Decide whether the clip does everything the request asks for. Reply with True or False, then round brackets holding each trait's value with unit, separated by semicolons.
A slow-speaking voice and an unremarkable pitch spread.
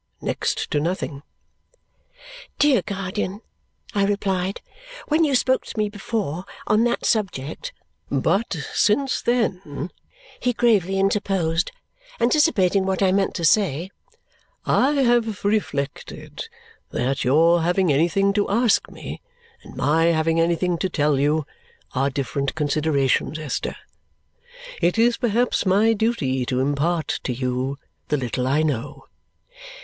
False (125 wpm; 6.2 semitones)